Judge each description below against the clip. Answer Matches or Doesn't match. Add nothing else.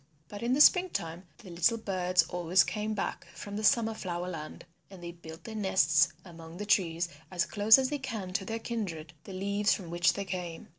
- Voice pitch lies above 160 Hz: Matches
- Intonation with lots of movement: Doesn't match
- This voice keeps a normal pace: Doesn't match